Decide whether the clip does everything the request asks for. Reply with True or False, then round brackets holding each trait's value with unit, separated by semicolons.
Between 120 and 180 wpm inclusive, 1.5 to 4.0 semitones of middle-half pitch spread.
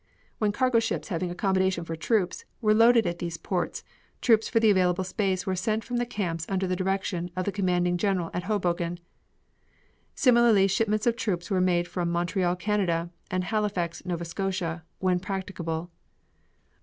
True (165 wpm; 3.1 semitones)